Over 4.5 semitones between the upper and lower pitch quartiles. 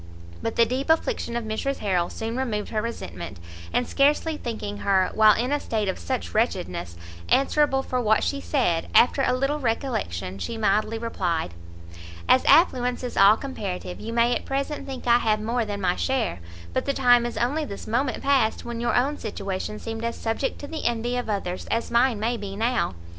No: average, 3.8 semitones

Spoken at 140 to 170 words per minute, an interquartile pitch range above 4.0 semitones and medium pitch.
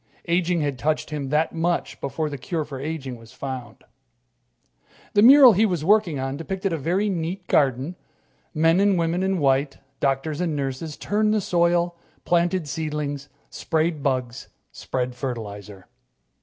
Yes: average, 150 wpm; average, 4.5 semitones; medium, 155 Hz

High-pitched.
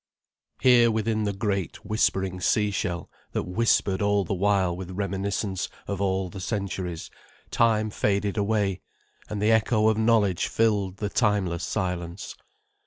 No: low, 100 Hz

